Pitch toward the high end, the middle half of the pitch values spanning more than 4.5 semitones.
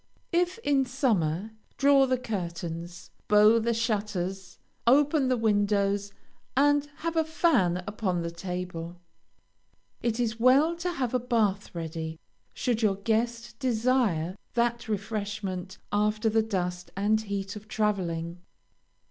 Yes: high, 215 Hz; average, 5.0 semitones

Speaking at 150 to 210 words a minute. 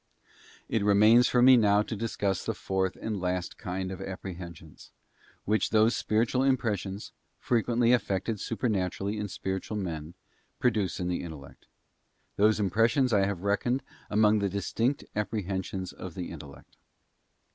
No: slow, 135 wpm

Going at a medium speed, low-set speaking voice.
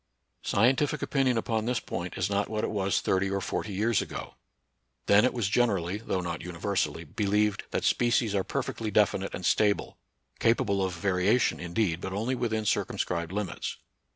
Yes: average, 175 wpm; low, 100 Hz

